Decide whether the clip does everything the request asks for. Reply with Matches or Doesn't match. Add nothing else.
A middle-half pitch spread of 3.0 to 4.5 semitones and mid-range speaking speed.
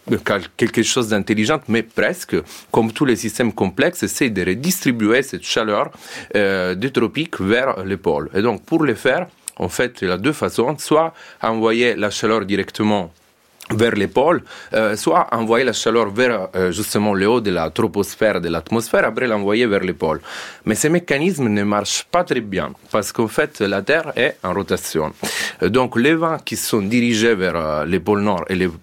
Matches